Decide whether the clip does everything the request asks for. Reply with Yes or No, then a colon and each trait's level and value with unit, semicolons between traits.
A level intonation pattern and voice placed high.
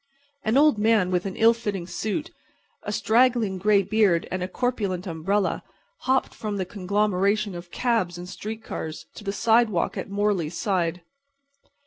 No: average, 3.4 semitones; high, 205 Hz